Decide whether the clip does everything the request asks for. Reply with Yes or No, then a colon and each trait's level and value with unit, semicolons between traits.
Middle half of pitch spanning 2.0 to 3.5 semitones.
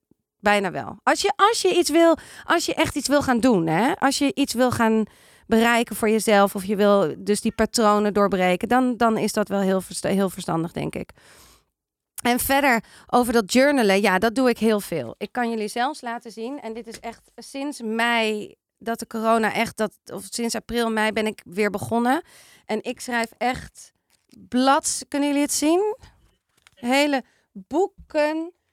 No: average, 4.2 semitones